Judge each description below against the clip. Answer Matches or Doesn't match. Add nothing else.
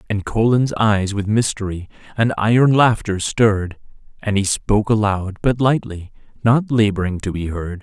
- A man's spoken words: Matches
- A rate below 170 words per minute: Matches